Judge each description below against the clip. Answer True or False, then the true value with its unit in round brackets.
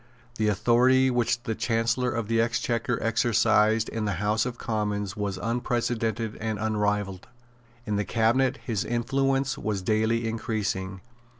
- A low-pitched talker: True (115 Hz)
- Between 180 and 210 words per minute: False (135 wpm)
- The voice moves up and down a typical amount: False (2.2 semitones)